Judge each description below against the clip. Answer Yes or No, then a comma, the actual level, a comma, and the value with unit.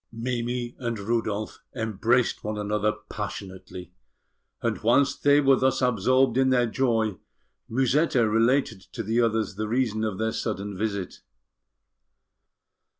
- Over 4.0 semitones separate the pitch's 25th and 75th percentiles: No, average, 2.9 semitones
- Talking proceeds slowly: Yes, slow, 125 wpm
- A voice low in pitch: Yes, low, 115 Hz